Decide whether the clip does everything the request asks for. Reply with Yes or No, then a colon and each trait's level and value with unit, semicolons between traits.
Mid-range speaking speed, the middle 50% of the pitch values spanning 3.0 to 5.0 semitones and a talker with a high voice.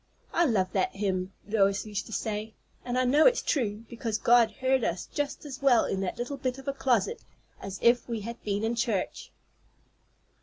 Yes: average, 195 wpm; average, 4.0 semitones; high, 230 Hz